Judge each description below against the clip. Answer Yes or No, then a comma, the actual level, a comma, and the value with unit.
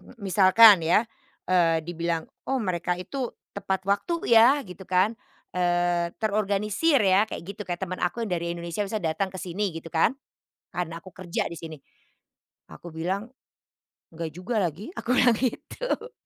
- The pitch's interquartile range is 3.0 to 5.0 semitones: Yes, average, 3.9 semitones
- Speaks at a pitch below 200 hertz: Yes, medium, 185 Hz